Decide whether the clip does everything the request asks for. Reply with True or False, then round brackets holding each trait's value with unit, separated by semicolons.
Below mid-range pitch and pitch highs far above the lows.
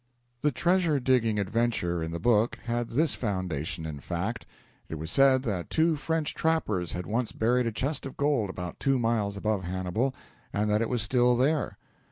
True (115 Hz; 6.0 semitones)